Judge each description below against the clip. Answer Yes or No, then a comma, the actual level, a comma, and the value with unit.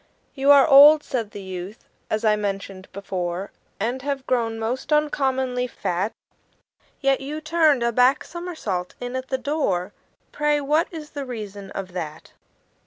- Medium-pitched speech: No, very high, 250 Hz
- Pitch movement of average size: No, wide, 6.2 semitones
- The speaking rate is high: No, average, 155 wpm